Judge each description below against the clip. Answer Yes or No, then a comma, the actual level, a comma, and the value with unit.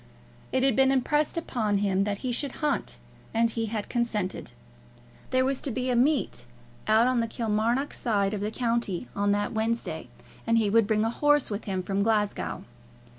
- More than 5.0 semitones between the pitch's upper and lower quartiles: No, average, 3.7 semitones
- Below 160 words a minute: No, average, 185 wpm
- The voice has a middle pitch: No, high, 230 Hz